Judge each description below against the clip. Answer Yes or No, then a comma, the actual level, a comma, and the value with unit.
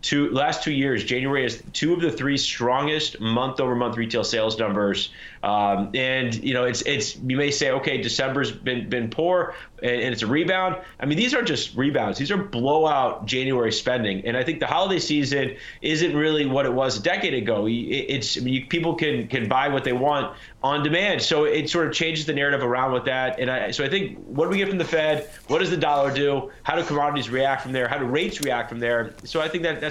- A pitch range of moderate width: Yes, average, 3.8 semitones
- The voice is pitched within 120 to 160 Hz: Yes, low, 135 Hz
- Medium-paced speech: No, fast, 235 wpm